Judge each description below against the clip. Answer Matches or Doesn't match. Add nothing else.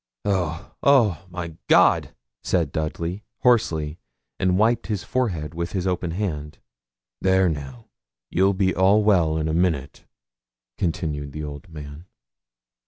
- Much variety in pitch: Doesn't match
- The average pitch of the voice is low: Matches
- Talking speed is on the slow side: Matches